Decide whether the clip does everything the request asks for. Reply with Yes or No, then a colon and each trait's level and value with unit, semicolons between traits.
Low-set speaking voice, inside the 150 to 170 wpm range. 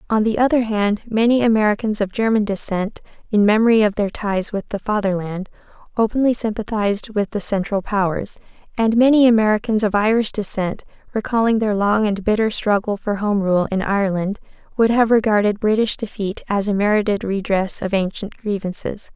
No: high, 210 Hz; average, 165 wpm